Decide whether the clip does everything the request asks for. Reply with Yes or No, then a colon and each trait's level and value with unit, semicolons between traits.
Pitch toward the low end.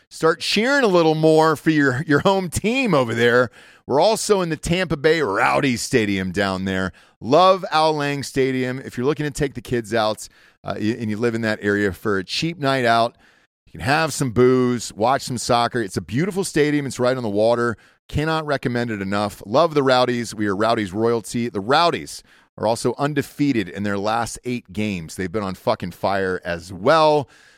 Yes: low, 125 Hz